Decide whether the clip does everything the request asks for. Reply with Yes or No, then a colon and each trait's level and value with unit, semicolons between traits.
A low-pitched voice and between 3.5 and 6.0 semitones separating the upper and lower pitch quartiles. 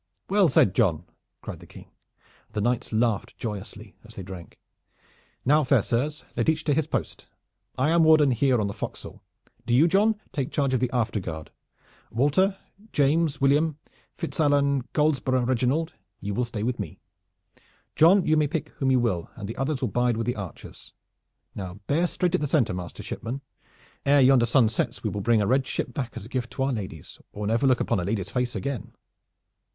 Yes: low, 130 Hz; average, 5.1 semitones